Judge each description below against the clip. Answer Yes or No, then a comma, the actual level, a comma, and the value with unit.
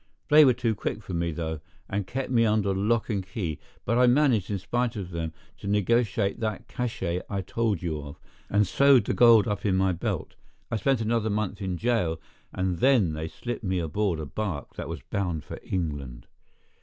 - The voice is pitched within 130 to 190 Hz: No, low, 100 Hz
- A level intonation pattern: No, average, 4.8 semitones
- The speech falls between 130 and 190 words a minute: No, average, 200 wpm